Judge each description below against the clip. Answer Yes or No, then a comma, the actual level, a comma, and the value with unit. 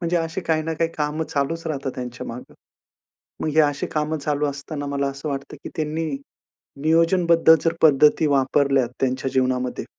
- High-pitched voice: No, medium, 150 Hz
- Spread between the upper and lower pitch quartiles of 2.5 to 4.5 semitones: Yes, average, 2.8 semitones